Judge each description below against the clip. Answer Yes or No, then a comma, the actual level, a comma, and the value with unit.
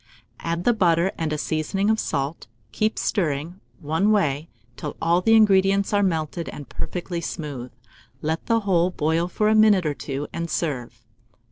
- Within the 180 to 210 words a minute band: No, average, 165 wpm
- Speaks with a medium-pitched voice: Yes, medium, 170 Hz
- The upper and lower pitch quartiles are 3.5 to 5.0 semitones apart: Yes, average, 4.4 semitones